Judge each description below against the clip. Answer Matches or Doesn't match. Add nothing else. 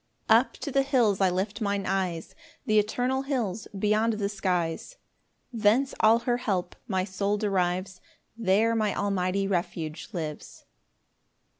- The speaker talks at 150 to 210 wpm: Doesn't match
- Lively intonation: Doesn't match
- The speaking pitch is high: Matches